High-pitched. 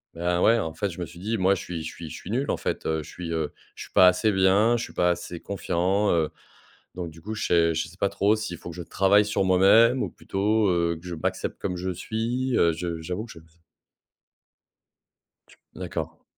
No: very low, 90 Hz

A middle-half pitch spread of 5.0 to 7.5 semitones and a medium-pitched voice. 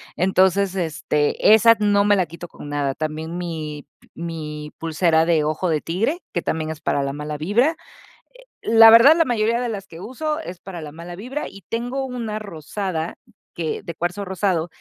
Yes: average, 5.3 semitones; medium, 175 Hz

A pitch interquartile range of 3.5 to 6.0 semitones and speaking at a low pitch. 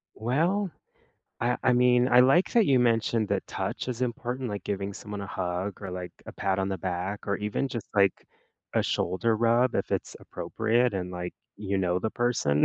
Yes: average, 4.3 semitones; low, 110 Hz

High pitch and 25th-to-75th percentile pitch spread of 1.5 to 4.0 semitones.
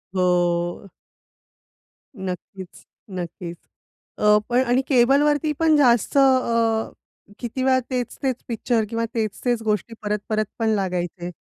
No: high, 225 Hz; average, 4.8 semitones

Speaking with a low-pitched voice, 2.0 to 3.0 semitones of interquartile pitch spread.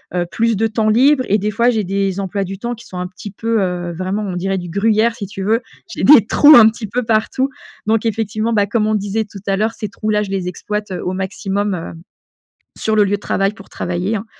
No: high, 210 Hz; narrow, 2.4 semitones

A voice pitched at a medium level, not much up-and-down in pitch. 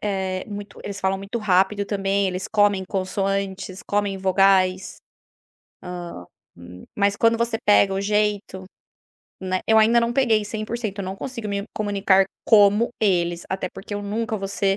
No: high, 200 Hz; narrow, 1.7 semitones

